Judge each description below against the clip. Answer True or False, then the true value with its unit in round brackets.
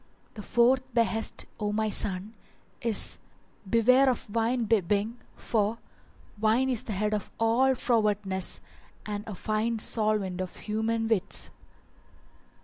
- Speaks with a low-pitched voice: False (220 Hz)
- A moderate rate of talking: False (125 wpm)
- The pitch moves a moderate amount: False (1.9 semitones)